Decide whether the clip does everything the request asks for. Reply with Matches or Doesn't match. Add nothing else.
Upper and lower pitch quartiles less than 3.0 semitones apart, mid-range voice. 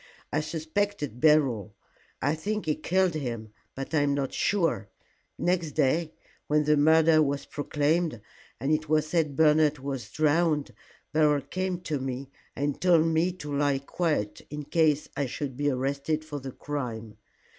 Matches